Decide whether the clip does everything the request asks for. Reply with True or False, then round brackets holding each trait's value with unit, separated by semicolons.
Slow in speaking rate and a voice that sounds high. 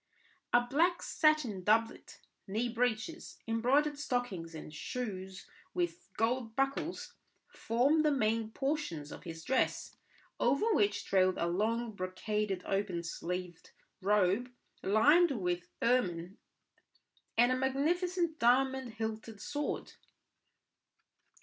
True (105 wpm; 225 Hz)